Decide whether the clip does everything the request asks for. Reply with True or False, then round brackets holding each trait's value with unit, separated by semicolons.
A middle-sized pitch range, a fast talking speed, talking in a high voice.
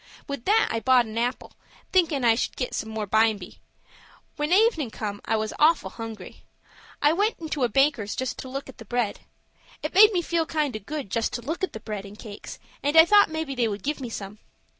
False (6.2 semitones; 225 wpm; 255 Hz)